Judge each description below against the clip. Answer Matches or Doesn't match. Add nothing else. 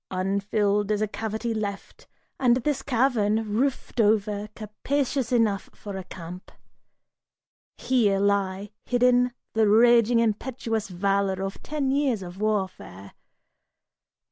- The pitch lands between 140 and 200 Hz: Doesn't match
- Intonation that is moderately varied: Matches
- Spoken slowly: Matches